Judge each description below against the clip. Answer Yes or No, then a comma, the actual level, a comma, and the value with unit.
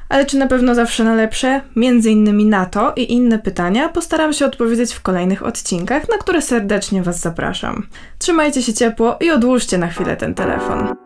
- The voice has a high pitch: Yes, high, 235 Hz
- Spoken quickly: Yes, fast, 185 wpm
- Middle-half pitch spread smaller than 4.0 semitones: No, average, 4.7 semitones